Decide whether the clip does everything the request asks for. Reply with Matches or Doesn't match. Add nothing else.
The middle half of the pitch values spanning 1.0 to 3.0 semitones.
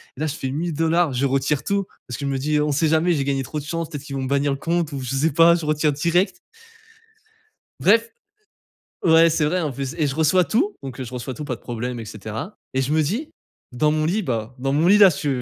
Doesn't match